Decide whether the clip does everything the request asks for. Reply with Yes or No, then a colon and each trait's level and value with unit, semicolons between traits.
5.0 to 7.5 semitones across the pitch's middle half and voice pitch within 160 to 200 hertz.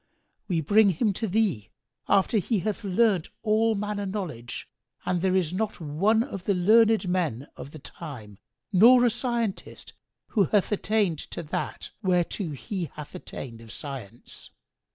Yes: wide, 5.6 semitones; high, 190 Hz